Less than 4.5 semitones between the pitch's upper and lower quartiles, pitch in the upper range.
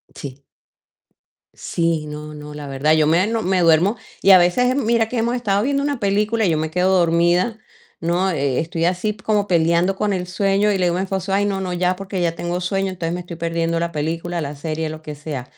No: average, 3.3 semitones; medium, 180 Hz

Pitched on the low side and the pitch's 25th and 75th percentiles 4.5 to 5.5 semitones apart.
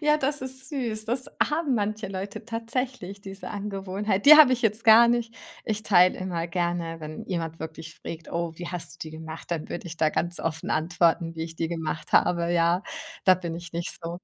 No: medium, 185 Hz; average, 5.0 semitones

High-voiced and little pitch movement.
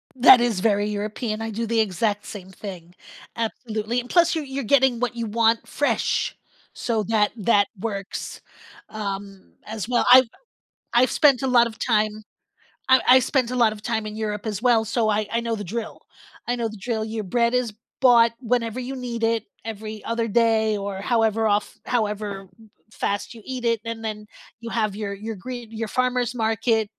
Yes: high, 225 Hz; narrow, 2.3 semitones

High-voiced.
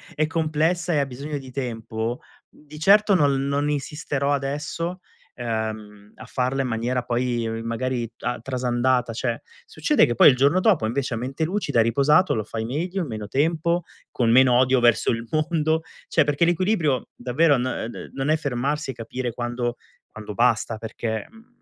No: low, 130 Hz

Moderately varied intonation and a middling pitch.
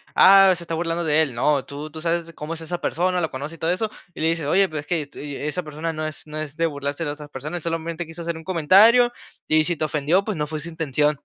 No: narrow, 2.3 semitones; medium, 160 Hz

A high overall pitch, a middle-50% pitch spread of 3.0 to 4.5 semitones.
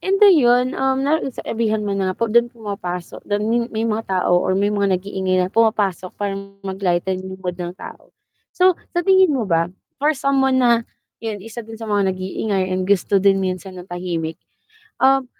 Yes: high, 205 Hz; average, 4.1 semitones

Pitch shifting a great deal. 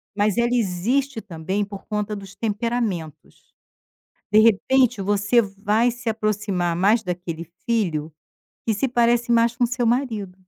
No: average, 3.3 semitones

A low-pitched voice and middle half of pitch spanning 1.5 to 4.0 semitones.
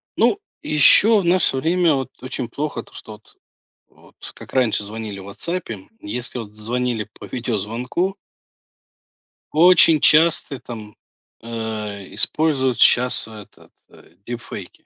No: low, 125 Hz; wide, 6.0 semitones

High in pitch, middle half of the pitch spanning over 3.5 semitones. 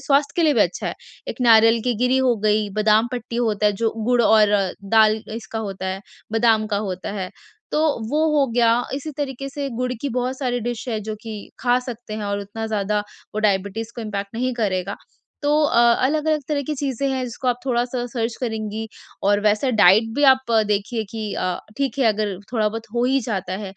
No: high, 225 Hz; average, 3.2 semitones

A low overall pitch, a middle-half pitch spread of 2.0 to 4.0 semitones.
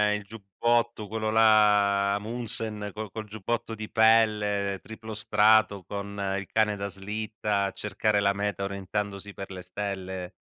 No: low, 105 Hz; narrow, 1.5 semitones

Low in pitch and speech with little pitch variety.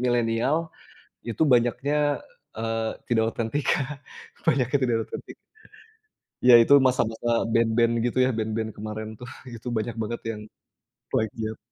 Yes: low, 115 Hz; narrow, 2.3 semitones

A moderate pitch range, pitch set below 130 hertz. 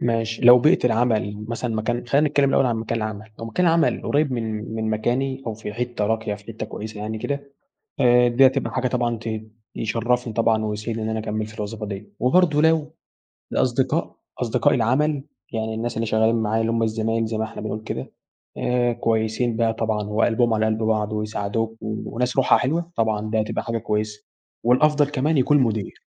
No: narrow, 2.3 semitones; low, 115 Hz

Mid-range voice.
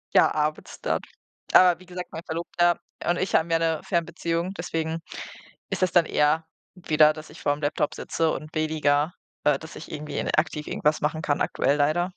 Yes: medium, 160 Hz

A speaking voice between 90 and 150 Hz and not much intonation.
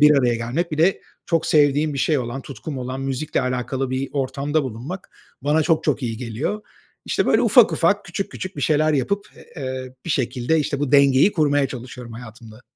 No: low, 135 Hz; average, 3.3 semitones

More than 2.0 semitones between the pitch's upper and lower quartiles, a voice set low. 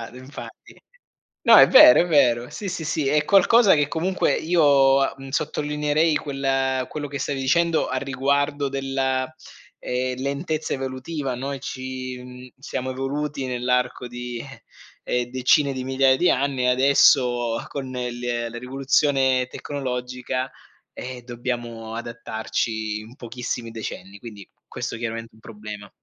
Yes: narrow, 2.5 semitones; low, 130 Hz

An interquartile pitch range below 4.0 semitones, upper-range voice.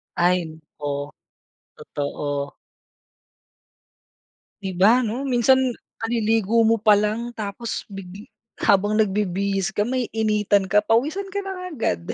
Yes: average, 3.6 semitones; high, 210 Hz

